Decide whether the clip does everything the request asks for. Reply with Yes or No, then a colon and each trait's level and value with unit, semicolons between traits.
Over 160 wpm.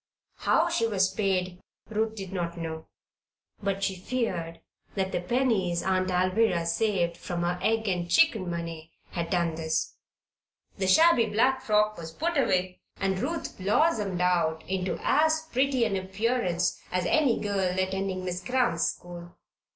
No: average, 150 wpm